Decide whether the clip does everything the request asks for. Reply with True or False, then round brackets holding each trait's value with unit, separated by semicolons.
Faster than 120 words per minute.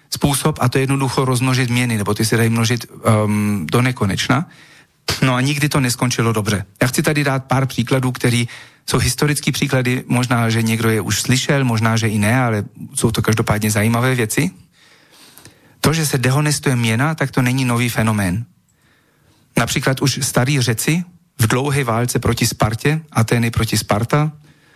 True (165 wpm)